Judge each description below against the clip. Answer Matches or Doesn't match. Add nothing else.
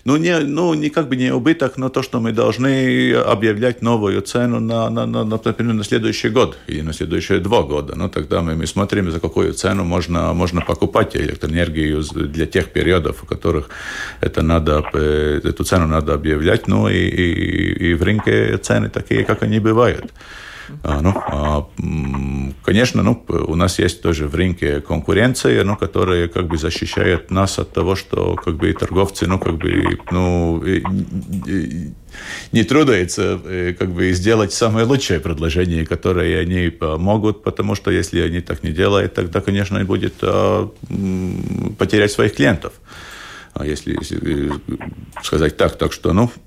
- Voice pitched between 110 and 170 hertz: Doesn't match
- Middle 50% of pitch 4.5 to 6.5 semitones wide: Matches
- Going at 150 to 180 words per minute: Matches